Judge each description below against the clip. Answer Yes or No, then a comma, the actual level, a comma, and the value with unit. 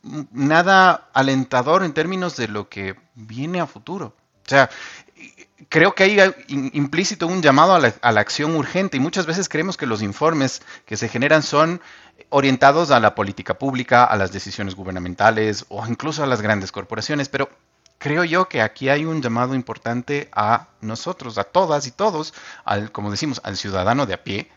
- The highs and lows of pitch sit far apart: Yes, wide, 6.3 semitones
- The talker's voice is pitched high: No, low, 135 Hz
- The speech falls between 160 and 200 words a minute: Yes, average, 180 wpm